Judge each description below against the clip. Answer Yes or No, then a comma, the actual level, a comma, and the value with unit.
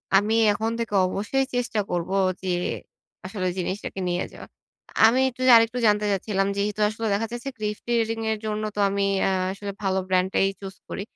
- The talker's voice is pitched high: Yes, high, 205 Hz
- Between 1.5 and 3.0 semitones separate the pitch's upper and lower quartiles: Yes, narrow, 2.6 semitones